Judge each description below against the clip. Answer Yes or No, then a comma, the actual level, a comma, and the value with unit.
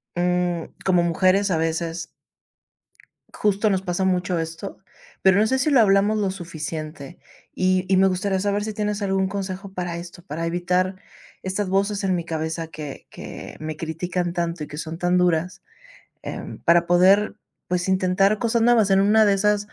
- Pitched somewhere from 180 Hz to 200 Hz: Yes, medium, 185 Hz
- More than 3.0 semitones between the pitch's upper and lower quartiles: No, narrow, 2.6 semitones